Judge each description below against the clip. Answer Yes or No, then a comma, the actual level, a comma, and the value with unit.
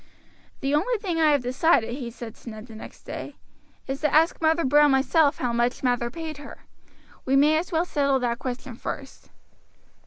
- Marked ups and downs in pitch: No, average, 4.2 semitones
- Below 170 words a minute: No, average, 190 wpm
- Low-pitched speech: No, very high, 275 Hz